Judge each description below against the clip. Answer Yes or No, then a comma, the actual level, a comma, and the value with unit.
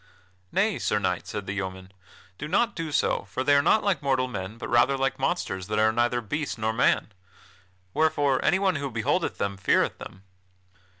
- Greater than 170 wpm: Yes, average, 185 wpm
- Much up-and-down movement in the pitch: Yes, wide, 6.3 semitones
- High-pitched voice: No, low, 130 Hz